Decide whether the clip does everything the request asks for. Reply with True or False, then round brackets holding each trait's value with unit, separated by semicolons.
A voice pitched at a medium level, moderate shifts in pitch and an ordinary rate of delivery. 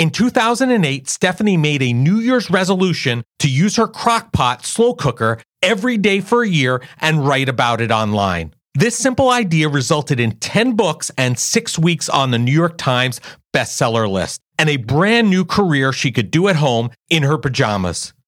False (150 Hz; 8.0 semitones; 180 wpm)